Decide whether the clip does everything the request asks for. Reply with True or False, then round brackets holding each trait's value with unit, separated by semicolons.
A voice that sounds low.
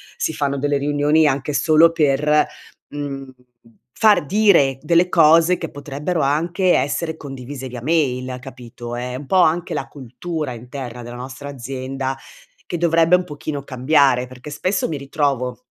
False (145 Hz)